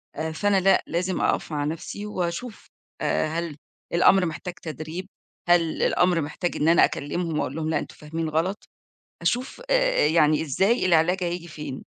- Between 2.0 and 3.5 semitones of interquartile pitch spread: Yes, average, 2.9 semitones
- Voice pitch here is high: No, medium, 170 Hz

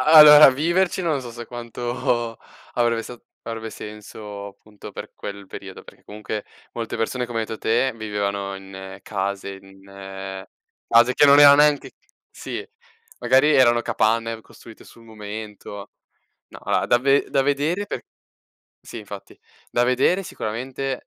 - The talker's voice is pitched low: Yes, low, 115 Hz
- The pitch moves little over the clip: No, average, 4.1 semitones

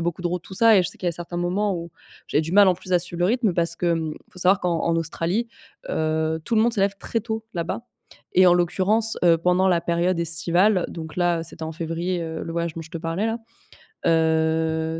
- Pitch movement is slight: Yes, narrow, 2.1 semitones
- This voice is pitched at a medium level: Yes, medium, 175 Hz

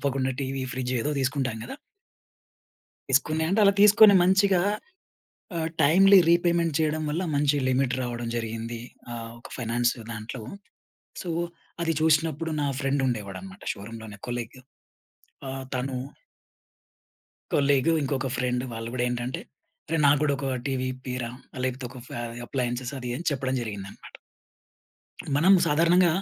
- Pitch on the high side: No, low, 135 Hz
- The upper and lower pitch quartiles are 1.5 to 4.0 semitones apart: No, average, 4.6 semitones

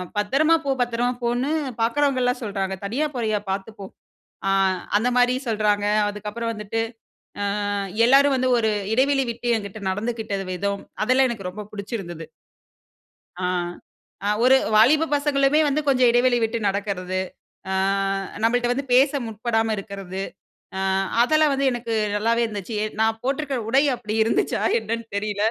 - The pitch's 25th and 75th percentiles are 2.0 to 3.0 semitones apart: No, average, 3.7 semitones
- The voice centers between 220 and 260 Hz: Yes, high, 230 Hz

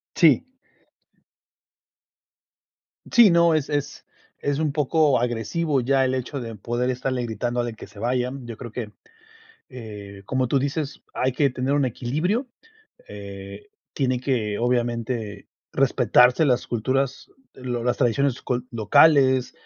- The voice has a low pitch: Yes, low, 125 Hz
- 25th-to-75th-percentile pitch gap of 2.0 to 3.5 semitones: Yes, average, 2.9 semitones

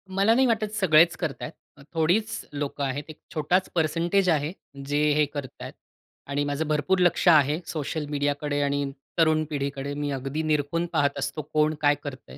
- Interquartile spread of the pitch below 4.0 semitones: Yes, narrow, 2.6 semitones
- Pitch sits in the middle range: Yes, medium, 150 Hz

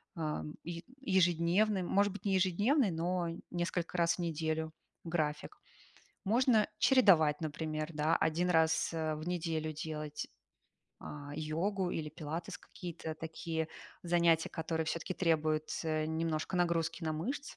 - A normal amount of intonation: No, narrow, 2.3 semitones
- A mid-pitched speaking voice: Yes, medium, 165 Hz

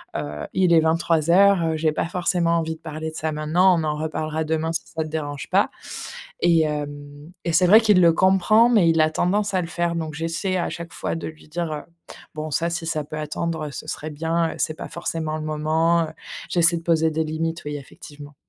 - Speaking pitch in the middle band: Yes, medium, 160 Hz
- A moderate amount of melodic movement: No, narrow, 1.7 semitones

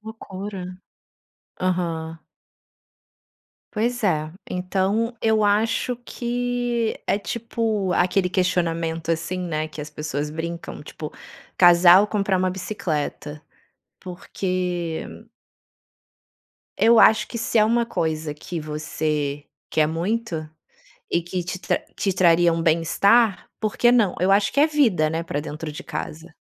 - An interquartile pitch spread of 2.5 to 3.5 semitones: No, average, 4.8 semitones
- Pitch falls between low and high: Yes, medium, 180 Hz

